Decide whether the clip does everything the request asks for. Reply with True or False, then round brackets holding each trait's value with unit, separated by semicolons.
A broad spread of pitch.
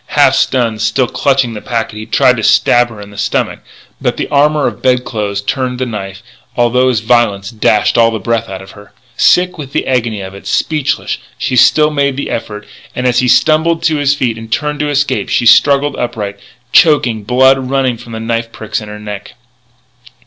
False (4.0 semitones)